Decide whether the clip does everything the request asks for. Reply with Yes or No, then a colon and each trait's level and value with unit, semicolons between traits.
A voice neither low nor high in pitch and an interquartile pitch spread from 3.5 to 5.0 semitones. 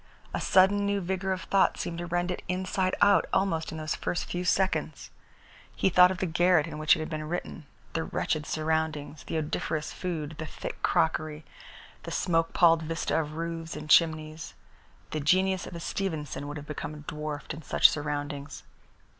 No: medium, 160 Hz; average, 2.8 semitones